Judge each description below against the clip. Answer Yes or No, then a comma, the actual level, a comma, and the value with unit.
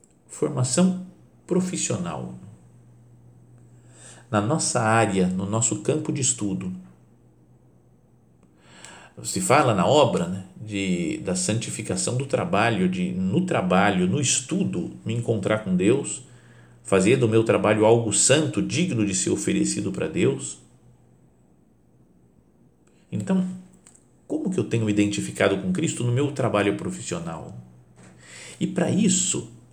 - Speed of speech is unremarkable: No, slow, 115 wpm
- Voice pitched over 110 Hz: No, low, 105 Hz